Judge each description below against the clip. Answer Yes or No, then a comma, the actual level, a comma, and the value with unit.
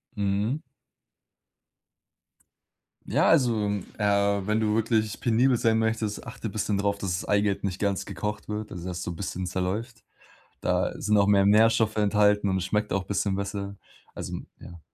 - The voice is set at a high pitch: No, low, 105 Hz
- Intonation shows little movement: Yes, narrow, 1.6 semitones